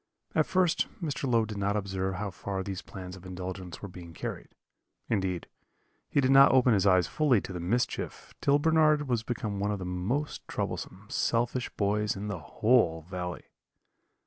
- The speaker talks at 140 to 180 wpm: Yes, average, 175 wpm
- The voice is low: Yes, low, 100 Hz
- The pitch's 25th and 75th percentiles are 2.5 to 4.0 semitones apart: No, average, 5.2 semitones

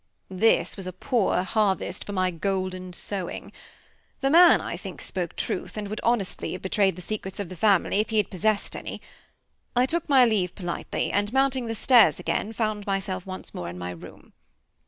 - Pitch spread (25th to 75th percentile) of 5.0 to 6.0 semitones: No, average, 3.2 semitones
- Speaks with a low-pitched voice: No, high, 200 Hz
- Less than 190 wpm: No, average, 195 wpm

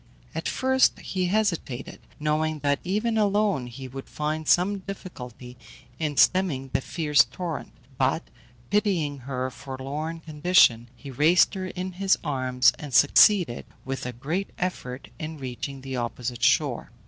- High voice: No, medium, 150 Hz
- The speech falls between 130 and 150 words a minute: Yes, average, 140 wpm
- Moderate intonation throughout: No, wide, 5.8 semitones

